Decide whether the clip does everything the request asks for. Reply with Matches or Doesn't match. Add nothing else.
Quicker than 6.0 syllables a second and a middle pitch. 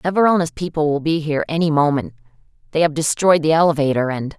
Matches